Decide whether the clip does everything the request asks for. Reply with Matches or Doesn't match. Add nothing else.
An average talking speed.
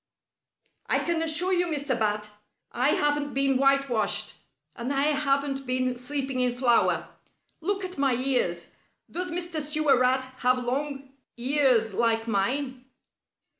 Doesn't match